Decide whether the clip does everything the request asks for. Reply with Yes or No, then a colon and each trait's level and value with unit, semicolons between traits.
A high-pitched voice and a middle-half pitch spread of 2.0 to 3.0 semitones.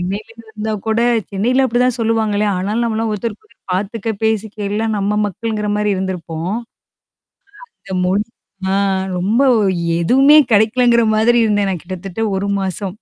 Yes: high, 210 Hz; average, 2.7 semitones